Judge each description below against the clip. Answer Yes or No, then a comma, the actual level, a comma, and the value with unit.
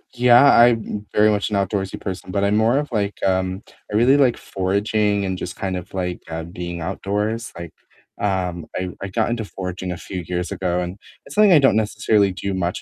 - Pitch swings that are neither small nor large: Yes, average, 3.2 semitones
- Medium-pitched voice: No, low, 100 Hz